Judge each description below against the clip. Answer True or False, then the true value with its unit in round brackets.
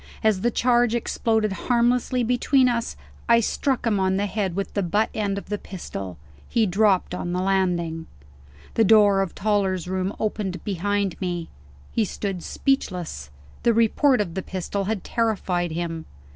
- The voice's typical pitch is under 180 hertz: False (200 Hz)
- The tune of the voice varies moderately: True (3.6 semitones)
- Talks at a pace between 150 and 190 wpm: True (160 wpm)